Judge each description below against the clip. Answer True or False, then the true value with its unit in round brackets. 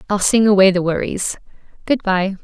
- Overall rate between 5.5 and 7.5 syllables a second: False (5.2 syllables/s)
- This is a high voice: True (195 Hz)